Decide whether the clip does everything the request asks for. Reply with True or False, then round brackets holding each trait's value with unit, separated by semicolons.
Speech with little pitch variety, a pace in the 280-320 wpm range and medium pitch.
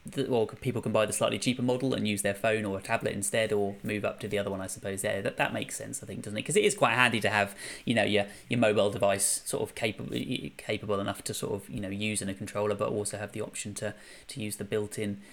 False (1.7 semitones; 285 wpm; 105 Hz)